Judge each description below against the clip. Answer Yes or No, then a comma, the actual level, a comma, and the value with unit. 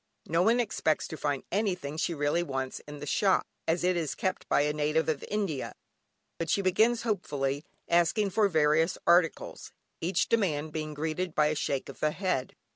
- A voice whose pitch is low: No, medium, 160 Hz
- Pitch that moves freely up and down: No, average, 3.9 semitones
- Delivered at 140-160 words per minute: No, average, 185 wpm